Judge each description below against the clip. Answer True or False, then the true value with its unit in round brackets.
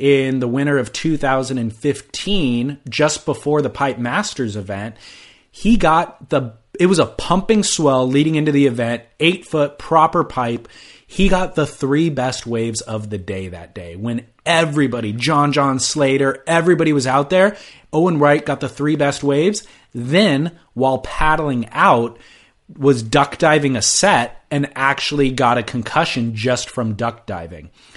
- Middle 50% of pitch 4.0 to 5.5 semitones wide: True (4.3 semitones)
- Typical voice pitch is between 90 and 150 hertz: True (140 Hz)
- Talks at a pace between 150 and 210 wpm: True (155 wpm)